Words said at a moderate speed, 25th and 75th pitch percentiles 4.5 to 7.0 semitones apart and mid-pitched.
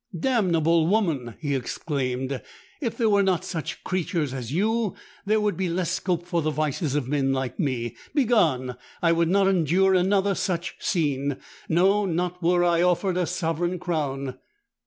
Yes: average, 155 wpm; average, 4.9 semitones; medium, 170 Hz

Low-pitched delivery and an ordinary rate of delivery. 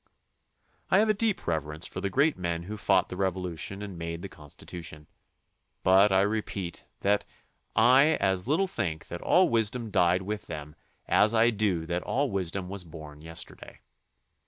Yes: very low, 95 Hz; average, 170 wpm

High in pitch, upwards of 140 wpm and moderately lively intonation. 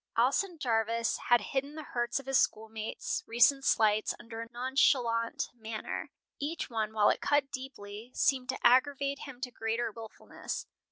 Yes: high, 240 Hz; average, 155 wpm; average, 3.3 semitones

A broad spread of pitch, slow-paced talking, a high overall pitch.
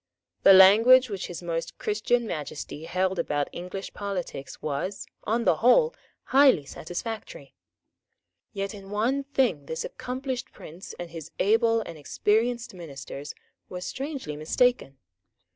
Yes: wide, 6.5 semitones; slow, 125 wpm; high, 195 Hz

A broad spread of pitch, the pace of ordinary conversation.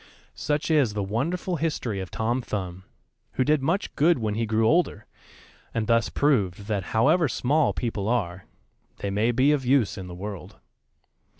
Yes: wide, 6.0 semitones; average, 170 wpm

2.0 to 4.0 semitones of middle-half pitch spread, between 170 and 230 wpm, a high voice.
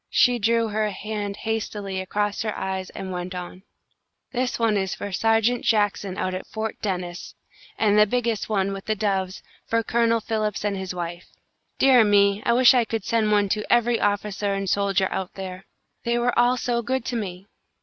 Yes: average, 3.0 semitones; average, 190 wpm; high, 210 Hz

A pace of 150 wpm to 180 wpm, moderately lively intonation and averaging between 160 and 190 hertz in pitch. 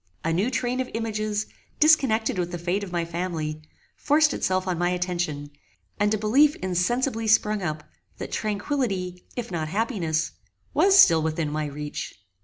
Yes: average, 160 wpm; average, 5.0 semitones; medium, 185 Hz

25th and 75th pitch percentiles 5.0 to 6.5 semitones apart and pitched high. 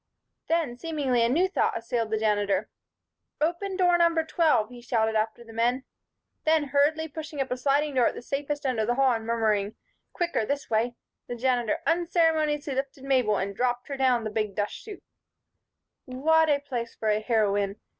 Yes: average, 5.3 semitones; very high, 255 Hz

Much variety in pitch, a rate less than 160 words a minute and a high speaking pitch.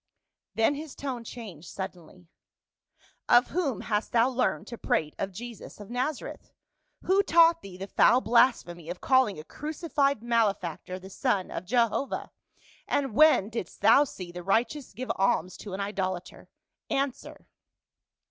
Yes: wide, 5.9 semitones; average, 150 wpm; high, 230 Hz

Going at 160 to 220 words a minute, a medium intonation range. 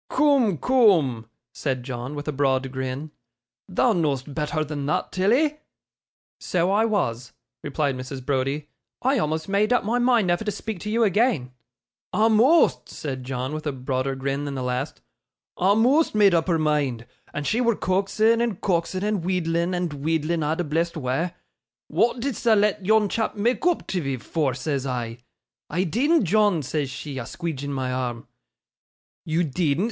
No: average, 170 wpm; wide, 7.5 semitones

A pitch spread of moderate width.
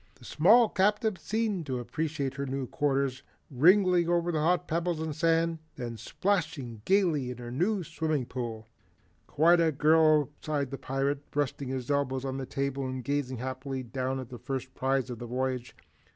Yes: average, 4.1 semitones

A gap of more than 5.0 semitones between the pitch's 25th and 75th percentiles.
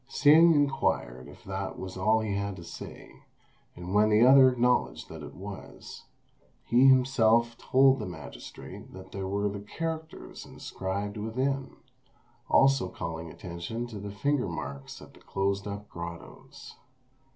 Yes: wide, 5.5 semitones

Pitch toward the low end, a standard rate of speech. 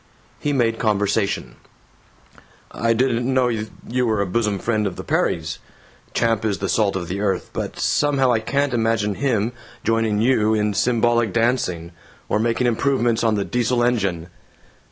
Yes: low, 115 Hz; average, 155 wpm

